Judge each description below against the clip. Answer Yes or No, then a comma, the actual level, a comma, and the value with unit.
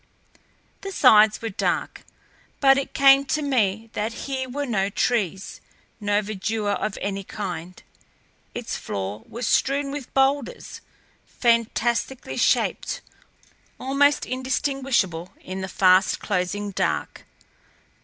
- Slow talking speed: Yes, slow, 115 wpm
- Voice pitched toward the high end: Yes, high, 225 Hz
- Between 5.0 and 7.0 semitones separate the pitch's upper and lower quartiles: Yes, wide, 5.6 semitones